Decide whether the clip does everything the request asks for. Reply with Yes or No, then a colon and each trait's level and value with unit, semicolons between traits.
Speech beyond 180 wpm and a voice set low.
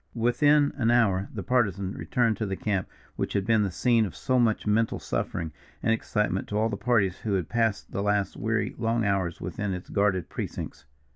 Yes: average, 200 wpm; low, 105 Hz